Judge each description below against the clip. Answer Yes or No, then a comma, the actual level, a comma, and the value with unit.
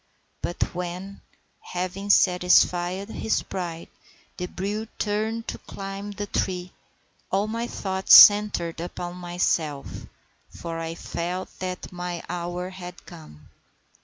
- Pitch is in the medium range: Yes, medium, 180 Hz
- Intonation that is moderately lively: No, narrow, 2.2 semitones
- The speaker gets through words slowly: Yes, slow, 115 wpm